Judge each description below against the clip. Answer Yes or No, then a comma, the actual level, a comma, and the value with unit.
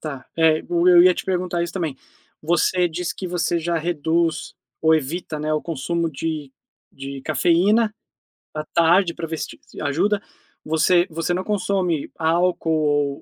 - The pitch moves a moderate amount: No, narrow, 2.3 semitones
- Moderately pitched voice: Yes, medium, 165 Hz